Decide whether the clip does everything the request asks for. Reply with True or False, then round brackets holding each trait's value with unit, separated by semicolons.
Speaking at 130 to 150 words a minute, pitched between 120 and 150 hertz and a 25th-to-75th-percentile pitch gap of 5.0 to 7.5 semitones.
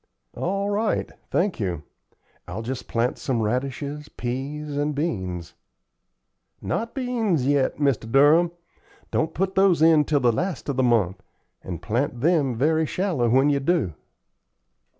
True (140 wpm; 140 Hz; 5.6 semitones)